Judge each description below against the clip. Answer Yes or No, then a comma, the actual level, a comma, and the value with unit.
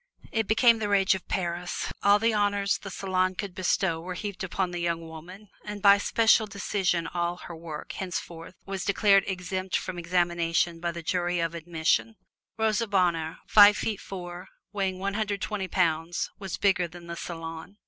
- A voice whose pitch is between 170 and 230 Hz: Yes, medium, 185 Hz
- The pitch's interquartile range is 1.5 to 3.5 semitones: Yes, average, 2.7 semitones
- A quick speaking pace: No, average, 175 wpm